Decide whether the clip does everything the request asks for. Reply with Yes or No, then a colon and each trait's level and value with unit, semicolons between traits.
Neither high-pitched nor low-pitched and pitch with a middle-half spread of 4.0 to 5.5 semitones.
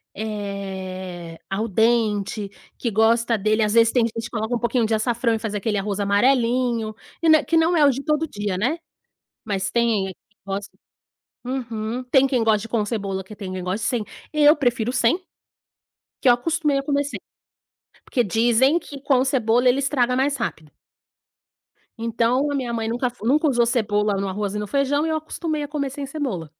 No: high, 235 Hz; average, 4.3 semitones